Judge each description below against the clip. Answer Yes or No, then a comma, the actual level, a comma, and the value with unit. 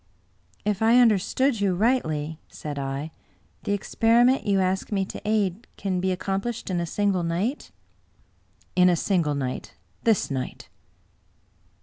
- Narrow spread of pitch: No, average, 4.5 semitones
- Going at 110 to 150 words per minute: No, average, 160 wpm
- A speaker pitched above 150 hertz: Yes, high, 190 Hz